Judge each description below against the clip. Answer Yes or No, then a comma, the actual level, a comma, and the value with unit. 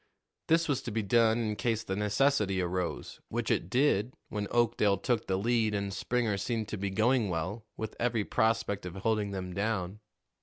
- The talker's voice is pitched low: Yes, low, 105 Hz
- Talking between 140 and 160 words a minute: No, average, 185 wpm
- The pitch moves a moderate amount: Yes, average, 3.0 semitones